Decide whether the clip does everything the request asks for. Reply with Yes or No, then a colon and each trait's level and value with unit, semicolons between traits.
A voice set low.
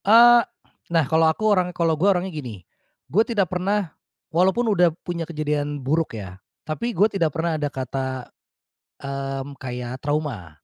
No: medium, 160 Hz